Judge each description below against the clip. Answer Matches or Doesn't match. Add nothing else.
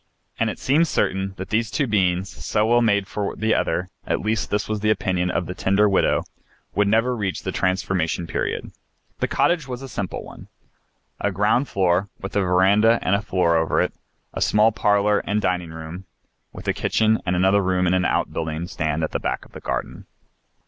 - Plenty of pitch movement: Doesn't match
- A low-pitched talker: Matches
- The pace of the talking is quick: Matches